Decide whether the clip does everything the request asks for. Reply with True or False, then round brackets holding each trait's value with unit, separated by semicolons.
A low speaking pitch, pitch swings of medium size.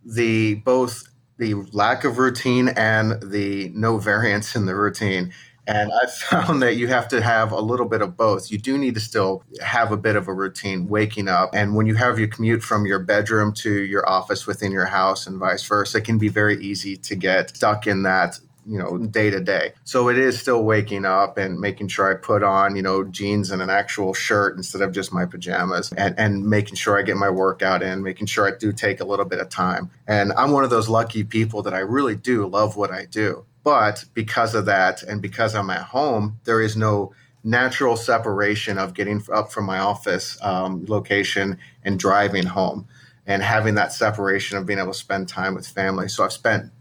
False (105 Hz; 2.3 semitones)